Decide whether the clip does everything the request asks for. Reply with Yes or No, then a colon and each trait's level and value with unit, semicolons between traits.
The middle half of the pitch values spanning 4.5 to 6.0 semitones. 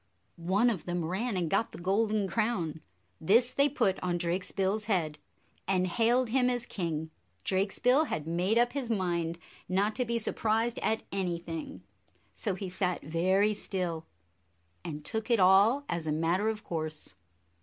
Yes: average, 4.8 semitones